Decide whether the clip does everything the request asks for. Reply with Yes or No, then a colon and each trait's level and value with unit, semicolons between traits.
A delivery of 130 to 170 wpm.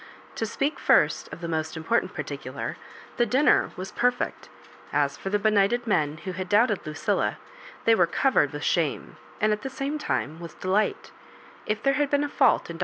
No: average, 190 wpm